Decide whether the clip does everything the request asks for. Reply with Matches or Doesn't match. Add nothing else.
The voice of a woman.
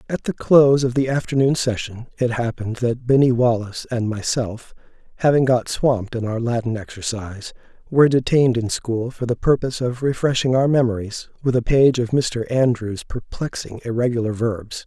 Doesn't match